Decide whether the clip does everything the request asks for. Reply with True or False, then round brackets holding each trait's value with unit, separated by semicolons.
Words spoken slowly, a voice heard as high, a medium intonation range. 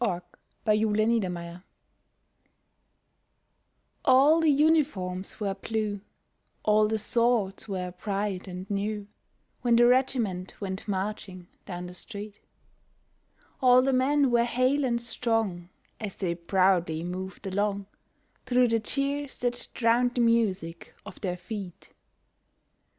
True (125 wpm; 210 Hz; 4.4 semitones)